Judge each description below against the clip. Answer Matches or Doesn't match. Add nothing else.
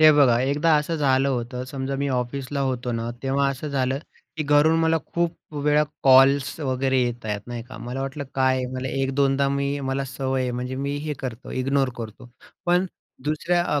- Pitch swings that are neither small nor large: Doesn't match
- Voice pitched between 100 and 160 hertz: Matches